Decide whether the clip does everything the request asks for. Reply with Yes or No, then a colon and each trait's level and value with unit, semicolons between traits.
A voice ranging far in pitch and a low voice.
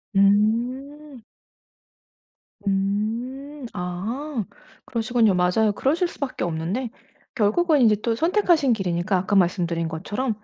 No: wide, 6.0 semitones; high, 220 Hz